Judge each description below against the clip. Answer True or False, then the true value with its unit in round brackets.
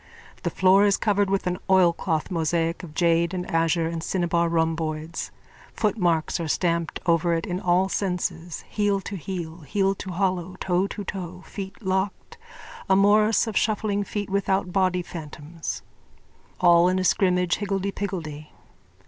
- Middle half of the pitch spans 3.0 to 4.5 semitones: False (2.6 semitones)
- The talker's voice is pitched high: False (180 Hz)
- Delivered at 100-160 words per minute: True (150 wpm)